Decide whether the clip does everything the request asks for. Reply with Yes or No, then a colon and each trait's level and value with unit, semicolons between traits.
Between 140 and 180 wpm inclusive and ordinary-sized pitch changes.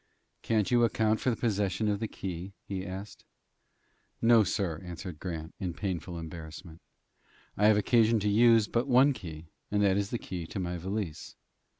Yes: average, 175 wpm; average, 3.9 semitones